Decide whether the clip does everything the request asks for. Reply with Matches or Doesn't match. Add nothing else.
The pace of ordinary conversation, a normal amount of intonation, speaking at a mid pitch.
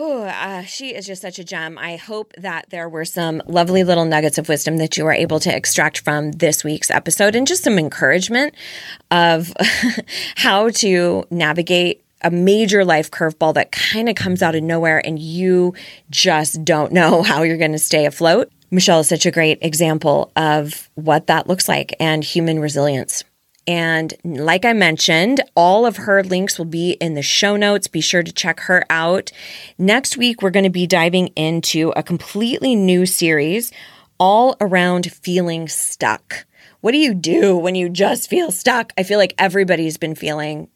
Matches